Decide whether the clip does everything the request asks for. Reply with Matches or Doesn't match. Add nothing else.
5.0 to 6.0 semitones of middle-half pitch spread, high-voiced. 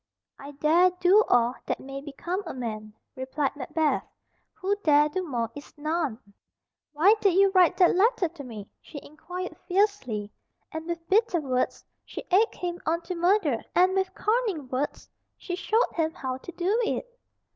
Matches